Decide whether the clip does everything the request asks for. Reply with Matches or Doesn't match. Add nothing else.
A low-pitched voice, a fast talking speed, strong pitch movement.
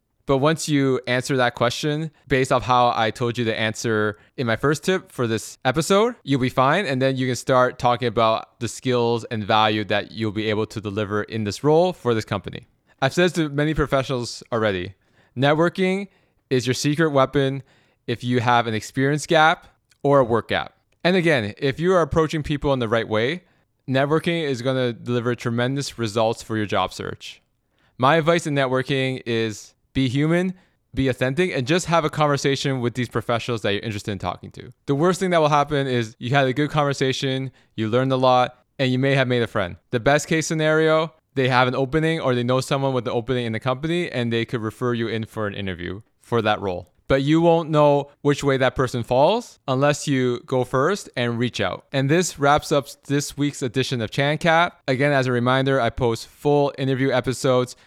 Doesn't match